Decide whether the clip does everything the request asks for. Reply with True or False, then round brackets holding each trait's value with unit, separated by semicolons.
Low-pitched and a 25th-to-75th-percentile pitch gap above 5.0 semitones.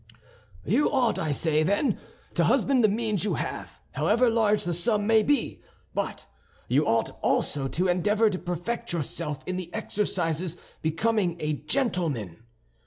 False (185 Hz; 5.4 semitones)